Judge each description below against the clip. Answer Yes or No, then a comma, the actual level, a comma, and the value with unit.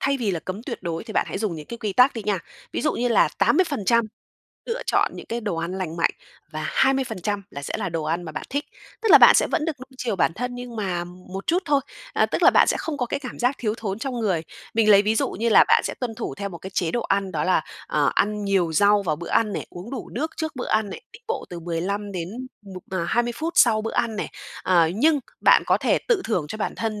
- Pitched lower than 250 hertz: Yes, high, 215 Hz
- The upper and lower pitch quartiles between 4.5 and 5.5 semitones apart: Yes, average, 5.0 semitones